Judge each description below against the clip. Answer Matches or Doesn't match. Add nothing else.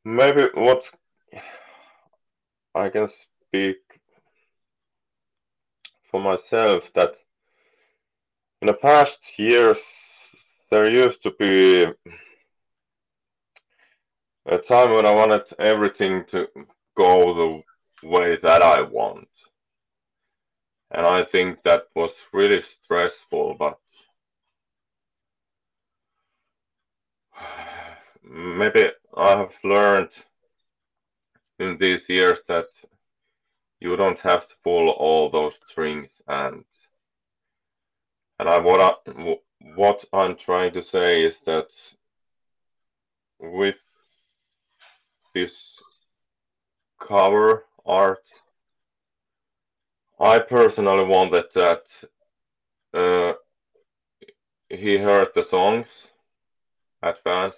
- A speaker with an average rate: Doesn't match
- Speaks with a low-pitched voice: Matches